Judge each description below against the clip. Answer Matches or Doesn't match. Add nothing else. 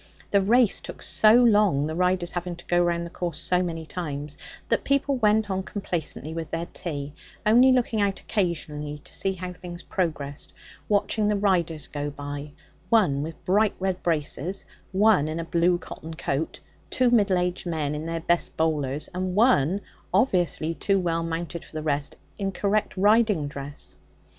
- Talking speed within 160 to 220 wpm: Matches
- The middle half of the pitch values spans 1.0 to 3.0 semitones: Doesn't match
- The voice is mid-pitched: Matches